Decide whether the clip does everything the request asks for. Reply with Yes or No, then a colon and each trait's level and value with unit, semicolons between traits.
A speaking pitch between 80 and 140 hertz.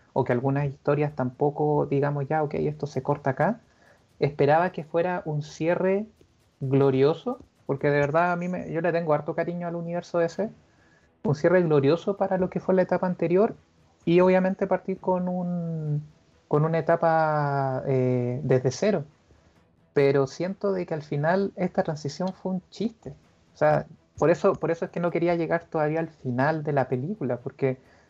No: medium, 160 Hz